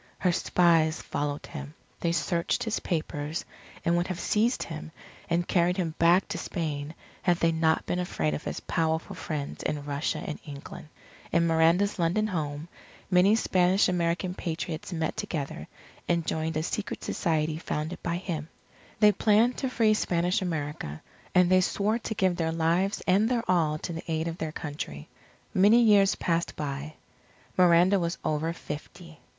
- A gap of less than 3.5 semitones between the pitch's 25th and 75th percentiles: Yes, average, 2.8 semitones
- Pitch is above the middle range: No, medium, 170 Hz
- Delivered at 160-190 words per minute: Yes, average, 165 wpm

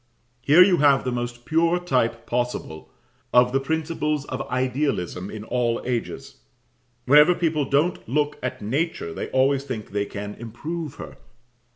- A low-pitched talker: Yes, low, 130 Hz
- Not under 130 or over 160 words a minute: Yes, average, 150 wpm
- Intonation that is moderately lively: Yes, average, 4.1 semitones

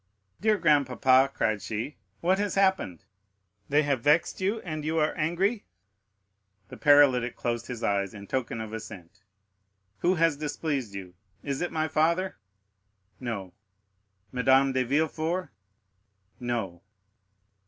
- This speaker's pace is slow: Yes, slow, 125 wpm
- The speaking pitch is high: No, medium, 140 Hz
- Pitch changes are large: Yes, wide, 5.8 semitones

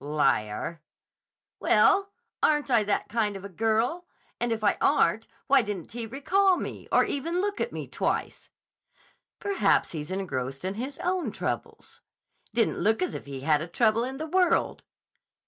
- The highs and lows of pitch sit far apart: Yes, wide, 9.0 semitones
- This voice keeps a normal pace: Yes, average, 165 wpm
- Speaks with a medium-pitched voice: No, high, 225 Hz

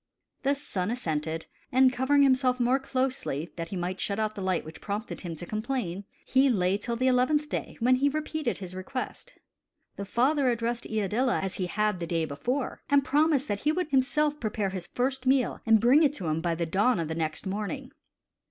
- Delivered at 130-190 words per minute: No, fast, 205 wpm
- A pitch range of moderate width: No, wide, 6.1 semitones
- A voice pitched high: Yes, high, 235 Hz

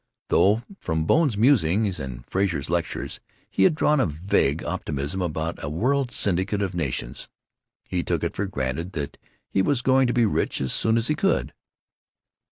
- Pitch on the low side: Yes, very low, 95 Hz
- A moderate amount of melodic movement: No, wide, 6.7 semitones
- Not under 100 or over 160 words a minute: No, average, 175 wpm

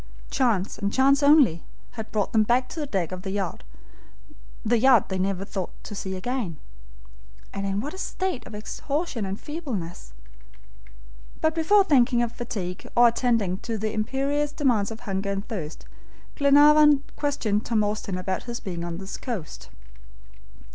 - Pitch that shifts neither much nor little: No, wide, 5.8 semitones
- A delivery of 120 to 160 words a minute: Yes, average, 155 wpm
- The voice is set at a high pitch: Yes, high, 225 Hz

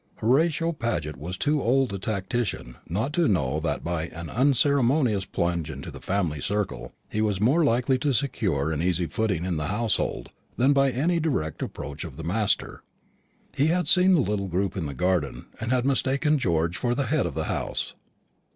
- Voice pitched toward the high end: No, low, 105 Hz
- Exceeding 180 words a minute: Yes, average, 190 wpm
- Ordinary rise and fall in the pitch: No, wide, 8.1 semitones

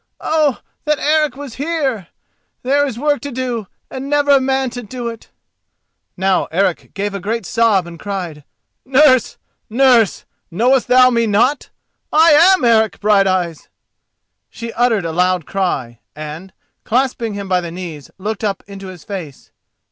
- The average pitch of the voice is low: No, high, 225 Hz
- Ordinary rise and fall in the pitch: No, wide, 5.9 semitones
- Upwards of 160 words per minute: No, average, 155 wpm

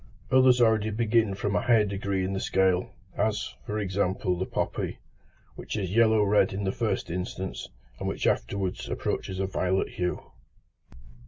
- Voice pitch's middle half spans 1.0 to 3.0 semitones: Yes, narrow, 2.5 semitones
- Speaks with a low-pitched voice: Yes, low, 100 Hz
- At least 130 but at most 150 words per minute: No, average, 160 wpm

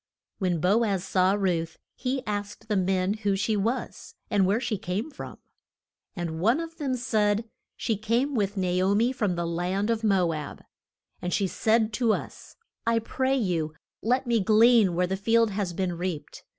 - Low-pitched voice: No, high, 205 Hz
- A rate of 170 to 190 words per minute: Yes, average, 185 wpm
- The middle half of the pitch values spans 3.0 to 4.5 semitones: Yes, average, 4.0 semitones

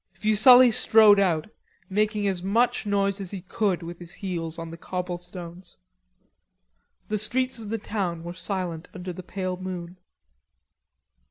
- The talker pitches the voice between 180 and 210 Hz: Yes, medium, 185 Hz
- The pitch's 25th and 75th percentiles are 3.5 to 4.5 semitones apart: No, average, 3.0 semitones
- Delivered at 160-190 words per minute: No, average, 150 wpm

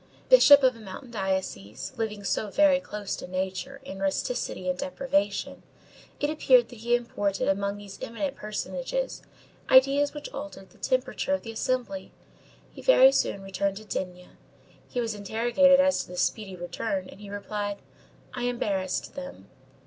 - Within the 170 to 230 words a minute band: No, average, 155 wpm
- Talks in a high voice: Yes, high, 220 Hz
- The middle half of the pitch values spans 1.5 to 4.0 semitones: No, wide, 5.6 semitones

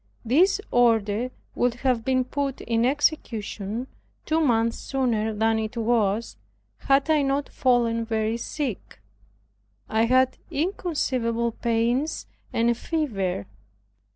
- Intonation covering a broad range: No, average, 3.3 semitones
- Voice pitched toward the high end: Yes, high, 235 Hz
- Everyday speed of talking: No, slow, 115 wpm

